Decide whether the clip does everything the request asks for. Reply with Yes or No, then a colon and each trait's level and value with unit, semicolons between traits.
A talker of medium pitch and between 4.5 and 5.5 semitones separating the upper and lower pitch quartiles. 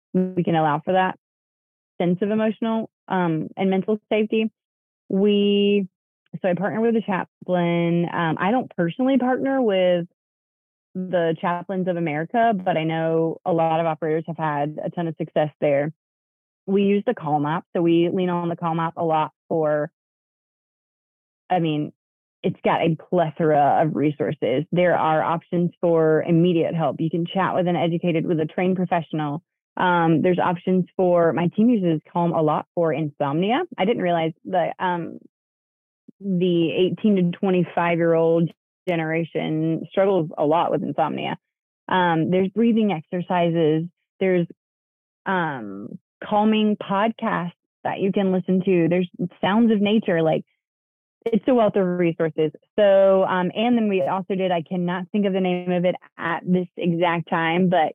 No: medium, 175 Hz; average, 2.8 semitones